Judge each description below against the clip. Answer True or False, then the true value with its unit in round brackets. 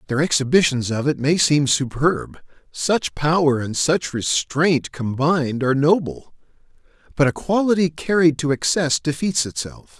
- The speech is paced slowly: True (125 wpm)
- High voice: False (150 Hz)